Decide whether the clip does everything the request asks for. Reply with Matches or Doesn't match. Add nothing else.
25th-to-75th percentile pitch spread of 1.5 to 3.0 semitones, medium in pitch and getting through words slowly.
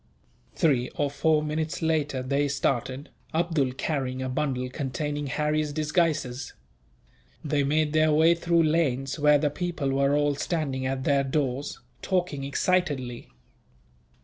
Matches